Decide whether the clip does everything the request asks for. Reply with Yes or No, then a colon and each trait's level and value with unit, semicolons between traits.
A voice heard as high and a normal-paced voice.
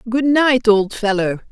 Yes: high, 225 Hz; average, 160 wpm